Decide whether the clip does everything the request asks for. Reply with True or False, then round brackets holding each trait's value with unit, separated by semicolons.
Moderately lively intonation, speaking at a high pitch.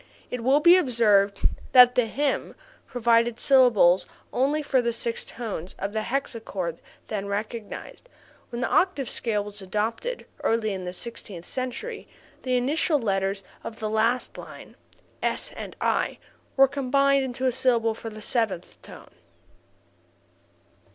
True (3.9 semitones; 235 Hz)